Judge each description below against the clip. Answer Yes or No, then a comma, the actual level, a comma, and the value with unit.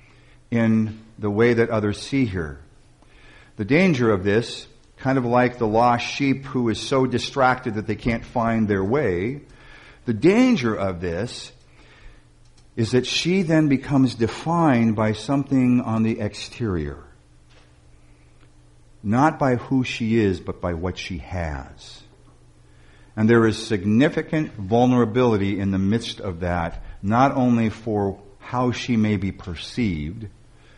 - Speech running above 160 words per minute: No, slow, 135 wpm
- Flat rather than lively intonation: No, average, 4.9 semitones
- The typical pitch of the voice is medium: No, low, 110 Hz